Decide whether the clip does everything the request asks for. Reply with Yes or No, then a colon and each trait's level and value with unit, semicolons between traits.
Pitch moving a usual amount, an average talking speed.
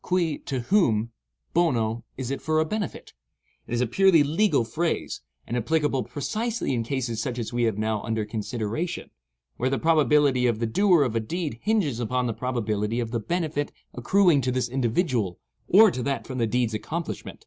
No: wide, 5.7 semitones; average, 185 wpm